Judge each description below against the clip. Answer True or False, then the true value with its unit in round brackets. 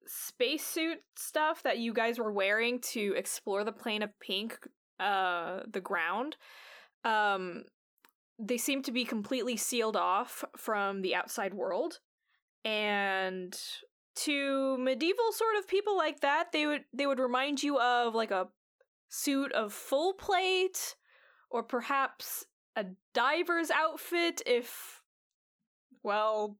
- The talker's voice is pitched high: True (255 Hz)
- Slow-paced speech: True (125 wpm)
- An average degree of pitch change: False (6.9 semitones)